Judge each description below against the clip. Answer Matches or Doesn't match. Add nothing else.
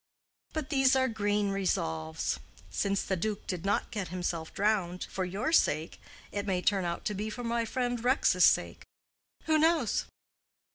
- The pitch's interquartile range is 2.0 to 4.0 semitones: Doesn't match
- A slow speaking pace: Doesn't match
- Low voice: Doesn't match